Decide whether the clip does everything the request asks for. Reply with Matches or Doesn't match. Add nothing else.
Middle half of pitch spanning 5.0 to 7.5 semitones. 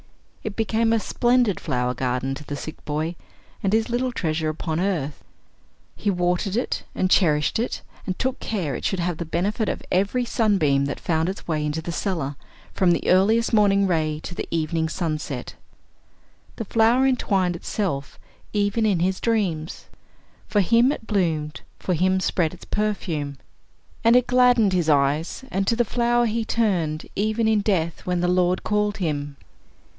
Matches